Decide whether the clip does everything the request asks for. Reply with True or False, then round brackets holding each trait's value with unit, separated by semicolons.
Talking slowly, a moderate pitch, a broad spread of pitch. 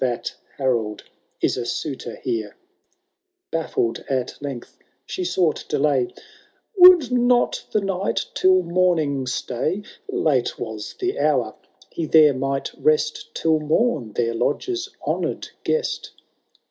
True (130 wpm; 150 Hz; 6.7 semitones)